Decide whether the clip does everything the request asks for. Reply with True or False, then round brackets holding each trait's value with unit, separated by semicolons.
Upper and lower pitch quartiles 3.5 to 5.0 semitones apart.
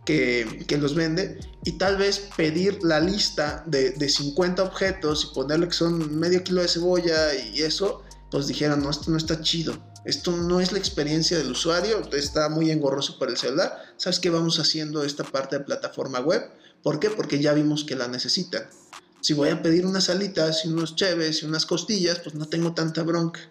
False (2.7 semitones)